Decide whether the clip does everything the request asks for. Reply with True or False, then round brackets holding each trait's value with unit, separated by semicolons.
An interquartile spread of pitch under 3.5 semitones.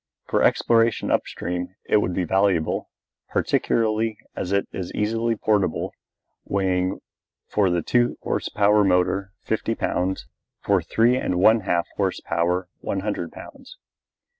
True (3.1 semitones)